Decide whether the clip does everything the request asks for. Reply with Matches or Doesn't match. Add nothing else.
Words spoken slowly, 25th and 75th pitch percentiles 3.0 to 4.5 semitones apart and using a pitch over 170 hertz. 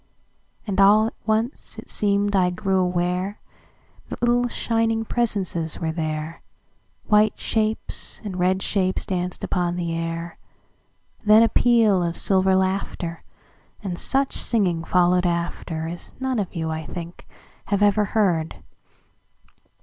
Matches